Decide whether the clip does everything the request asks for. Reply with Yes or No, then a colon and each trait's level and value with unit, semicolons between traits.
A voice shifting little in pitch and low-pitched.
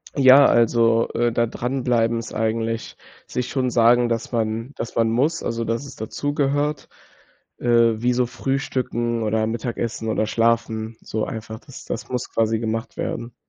Yes: narrow, 1.7 semitones; low, 115 Hz